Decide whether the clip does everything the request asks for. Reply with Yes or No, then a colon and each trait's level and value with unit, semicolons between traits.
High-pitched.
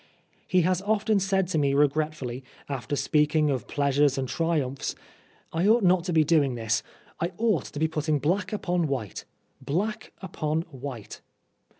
No: medium, 155 Hz